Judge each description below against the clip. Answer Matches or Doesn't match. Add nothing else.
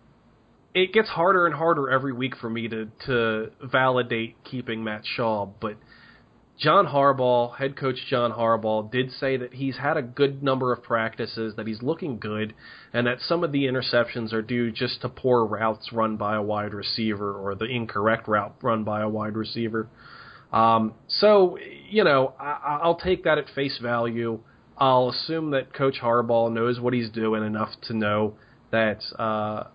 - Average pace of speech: Matches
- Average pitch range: Matches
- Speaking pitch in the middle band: Doesn't match